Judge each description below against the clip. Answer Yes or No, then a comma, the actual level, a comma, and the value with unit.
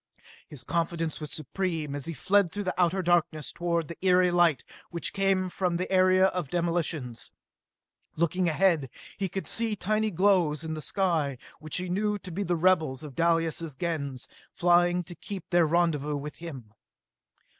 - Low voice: No, medium, 170 Hz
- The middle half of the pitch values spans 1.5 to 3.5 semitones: Yes, average, 3.0 semitones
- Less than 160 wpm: No, average, 165 wpm